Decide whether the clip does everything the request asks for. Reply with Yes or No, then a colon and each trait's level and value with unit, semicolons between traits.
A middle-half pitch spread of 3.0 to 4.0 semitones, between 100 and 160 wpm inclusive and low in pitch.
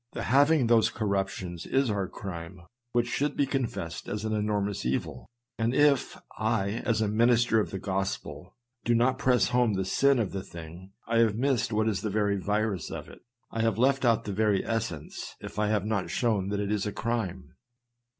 No: average, 3.3 semitones; average, 200 wpm; low, 110 Hz